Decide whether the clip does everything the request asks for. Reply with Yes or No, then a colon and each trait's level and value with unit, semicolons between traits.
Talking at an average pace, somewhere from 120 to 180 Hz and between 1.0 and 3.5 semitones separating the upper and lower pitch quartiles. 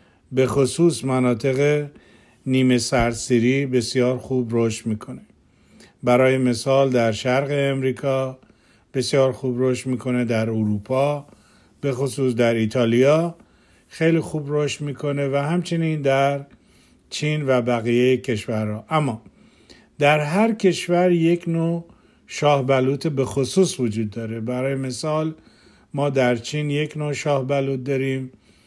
Yes: average, 120 wpm; low, 135 Hz; average, 2.9 semitones